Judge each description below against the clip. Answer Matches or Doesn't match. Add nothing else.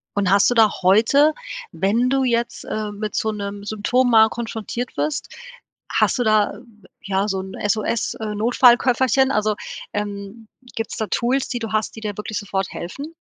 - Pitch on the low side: Doesn't match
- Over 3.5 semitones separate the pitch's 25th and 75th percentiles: Doesn't match